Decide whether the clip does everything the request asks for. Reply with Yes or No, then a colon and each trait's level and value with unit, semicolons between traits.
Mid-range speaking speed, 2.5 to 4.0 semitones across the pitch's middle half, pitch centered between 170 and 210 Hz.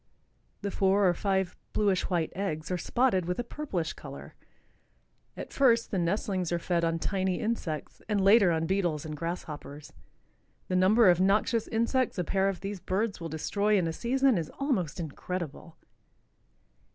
Yes: average, 165 wpm; average, 3.7 semitones; high, 190 Hz